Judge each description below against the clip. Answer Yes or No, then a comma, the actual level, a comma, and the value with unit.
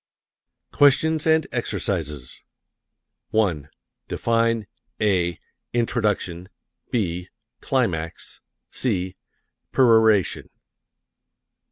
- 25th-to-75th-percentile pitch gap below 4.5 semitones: No, average, 5.2 semitones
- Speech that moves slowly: Yes, slow, 55 wpm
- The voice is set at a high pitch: No, low, 105 Hz